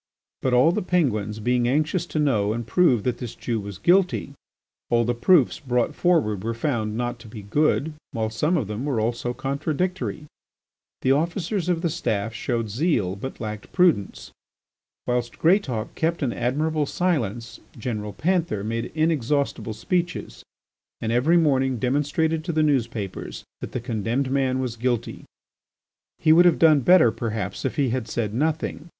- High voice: No, low, 130 Hz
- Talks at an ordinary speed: Yes, average, 160 wpm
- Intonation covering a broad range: Yes, wide, 5.7 semitones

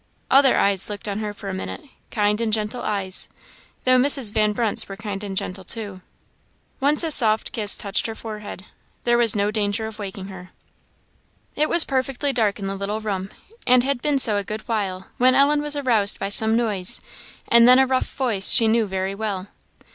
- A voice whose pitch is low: No, high, 215 Hz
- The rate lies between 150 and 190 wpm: No, average, 200 wpm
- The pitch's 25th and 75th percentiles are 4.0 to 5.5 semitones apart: No, average, 3.6 semitones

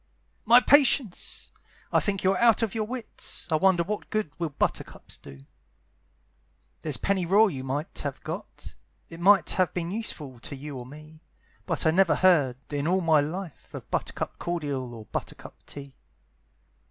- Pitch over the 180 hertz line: No, medium, 170 Hz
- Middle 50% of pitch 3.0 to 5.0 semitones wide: No, wide, 5.4 semitones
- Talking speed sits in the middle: Yes, average, 165 wpm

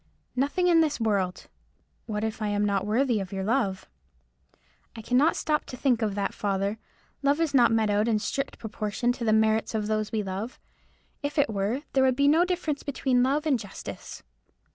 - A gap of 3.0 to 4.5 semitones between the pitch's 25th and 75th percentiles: No, average, 5.0 semitones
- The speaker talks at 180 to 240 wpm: Yes, average, 195 wpm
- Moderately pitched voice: No, high, 225 Hz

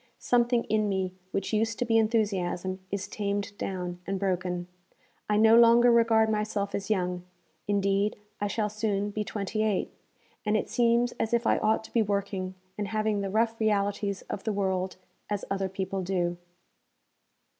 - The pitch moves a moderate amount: No, narrow, 2.3 semitones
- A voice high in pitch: Yes, high, 205 Hz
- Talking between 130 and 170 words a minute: Yes, average, 165 wpm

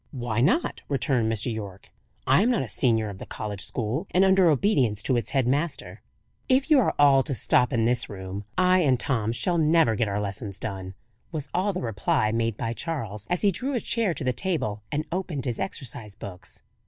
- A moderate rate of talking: No, fast, 210 wpm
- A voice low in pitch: Yes, low, 125 Hz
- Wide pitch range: Yes, wide, 7.6 semitones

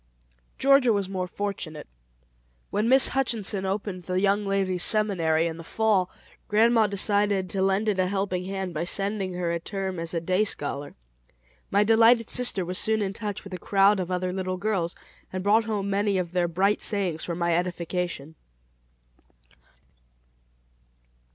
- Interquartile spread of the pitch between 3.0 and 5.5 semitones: No, narrow, 2.5 semitones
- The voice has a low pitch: No, high, 195 Hz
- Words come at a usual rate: Yes, average, 160 wpm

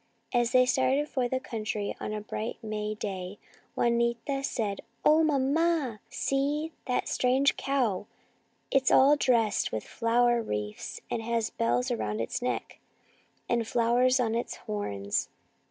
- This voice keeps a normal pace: Yes, average, 160 wpm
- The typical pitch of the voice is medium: No, high, 235 Hz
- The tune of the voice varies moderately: Yes, average, 3.8 semitones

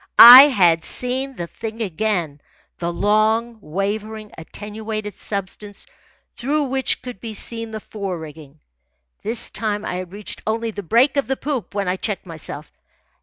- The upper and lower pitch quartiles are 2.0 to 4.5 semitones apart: Yes, average, 3.9 semitones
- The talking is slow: No, average, 155 wpm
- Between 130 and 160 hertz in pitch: No, high, 210 Hz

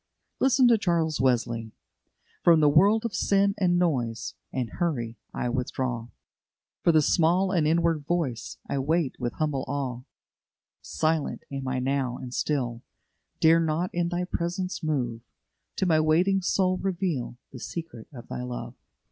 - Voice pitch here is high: No, medium, 155 Hz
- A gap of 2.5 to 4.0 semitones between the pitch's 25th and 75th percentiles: No, wide, 5.6 semitones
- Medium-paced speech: Yes, average, 150 wpm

